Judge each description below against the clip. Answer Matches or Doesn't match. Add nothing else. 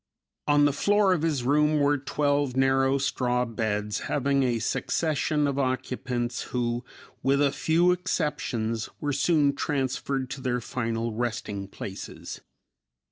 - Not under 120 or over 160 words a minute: Matches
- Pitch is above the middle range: Doesn't match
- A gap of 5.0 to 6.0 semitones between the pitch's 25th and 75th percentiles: Doesn't match